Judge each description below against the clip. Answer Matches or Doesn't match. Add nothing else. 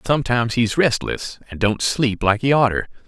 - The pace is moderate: Matches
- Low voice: Matches